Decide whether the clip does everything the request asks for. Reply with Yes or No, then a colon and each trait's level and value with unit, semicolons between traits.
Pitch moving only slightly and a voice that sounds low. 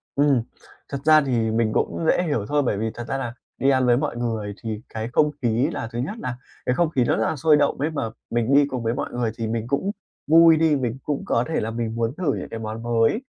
No: average, 4.2 semitones; low, 125 Hz